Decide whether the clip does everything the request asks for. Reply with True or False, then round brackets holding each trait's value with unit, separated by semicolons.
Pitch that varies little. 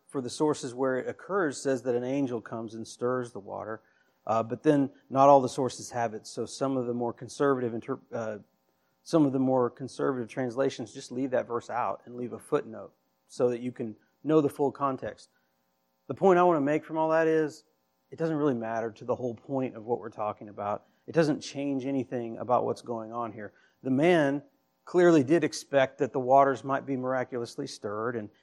False (3.4 semitones)